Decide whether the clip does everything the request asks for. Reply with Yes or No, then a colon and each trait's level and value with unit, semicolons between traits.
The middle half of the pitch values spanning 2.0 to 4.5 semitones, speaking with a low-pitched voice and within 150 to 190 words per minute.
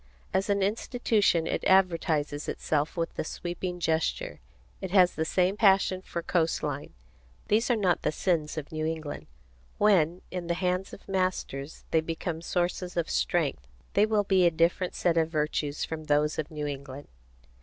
No: average, 3.2 semitones; medium, 170 Hz; average, 170 wpm